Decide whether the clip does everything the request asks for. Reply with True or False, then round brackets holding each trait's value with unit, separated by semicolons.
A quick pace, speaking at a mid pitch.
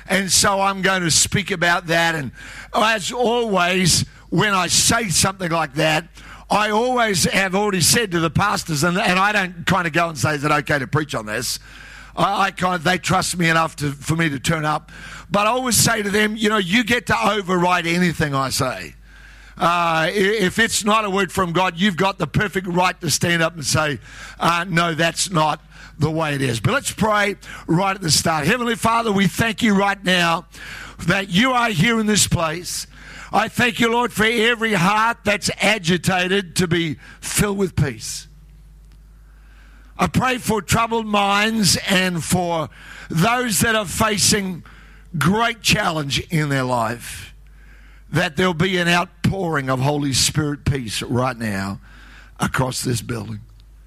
False (180 wpm; 180 Hz)